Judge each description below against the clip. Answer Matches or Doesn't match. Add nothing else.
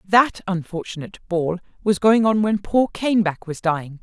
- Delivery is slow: Doesn't match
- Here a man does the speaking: Doesn't match